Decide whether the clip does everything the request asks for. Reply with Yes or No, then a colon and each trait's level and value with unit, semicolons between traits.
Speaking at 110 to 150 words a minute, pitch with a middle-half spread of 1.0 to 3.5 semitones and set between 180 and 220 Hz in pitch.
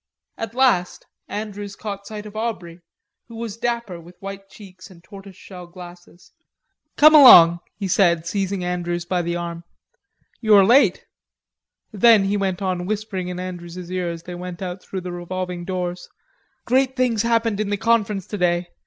No: average, 165 wpm; average, 3.2 semitones; high, 190 Hz